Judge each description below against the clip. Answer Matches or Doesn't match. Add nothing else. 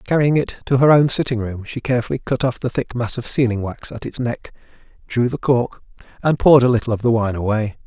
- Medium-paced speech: Doesn't match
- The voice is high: Doesn't match